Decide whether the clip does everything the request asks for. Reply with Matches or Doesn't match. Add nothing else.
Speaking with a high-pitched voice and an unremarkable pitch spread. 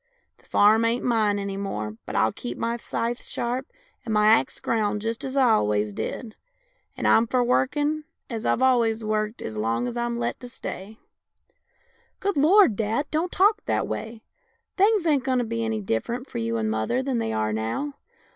Matches